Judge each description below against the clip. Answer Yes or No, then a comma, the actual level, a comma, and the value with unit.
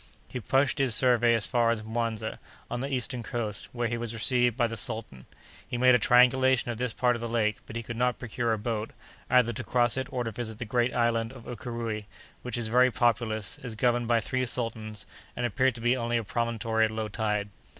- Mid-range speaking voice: No, low, 120 Hz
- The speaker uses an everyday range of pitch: No, narrow, 1.8 semitones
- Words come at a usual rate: No, fast, 225 wpm